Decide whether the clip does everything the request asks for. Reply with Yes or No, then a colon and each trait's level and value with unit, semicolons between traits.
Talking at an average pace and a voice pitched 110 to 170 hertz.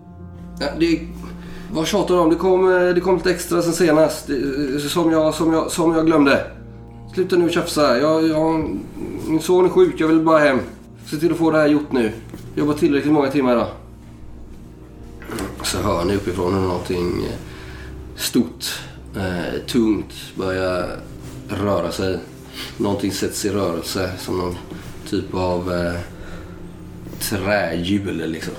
Yes: average, 150 wpm; medium, 140 Hz